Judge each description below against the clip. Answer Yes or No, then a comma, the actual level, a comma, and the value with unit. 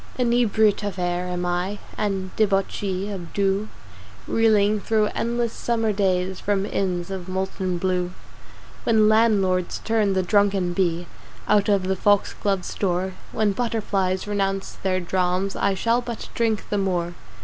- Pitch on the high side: Yes, high, 195 Hz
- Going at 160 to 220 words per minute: No, average, 140 wpm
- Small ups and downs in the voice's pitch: Yes, narrow, 2.3 semitones